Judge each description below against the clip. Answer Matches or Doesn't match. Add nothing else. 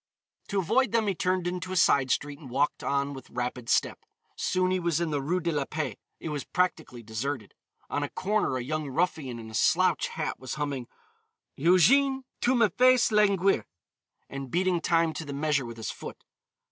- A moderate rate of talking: Matches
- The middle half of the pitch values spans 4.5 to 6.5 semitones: Matches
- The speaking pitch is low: Doesn't match